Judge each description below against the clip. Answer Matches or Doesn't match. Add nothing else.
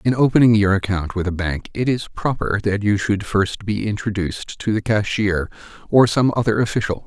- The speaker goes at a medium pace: Matches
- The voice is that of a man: Matches